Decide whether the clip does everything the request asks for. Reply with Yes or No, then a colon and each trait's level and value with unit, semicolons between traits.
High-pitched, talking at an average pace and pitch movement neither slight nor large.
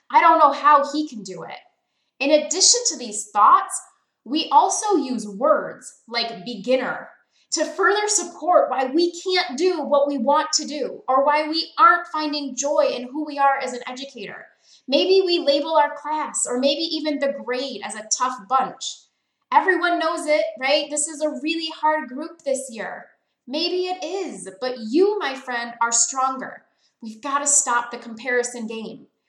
Yes: very high, 290 Hz; average, 175 wpm; average, 4.2 semitones